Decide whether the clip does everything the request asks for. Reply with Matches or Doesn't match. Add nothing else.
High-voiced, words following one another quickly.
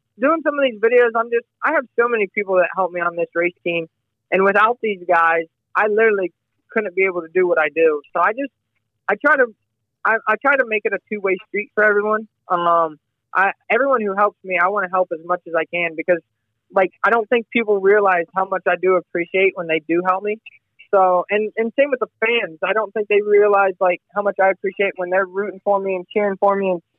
Matches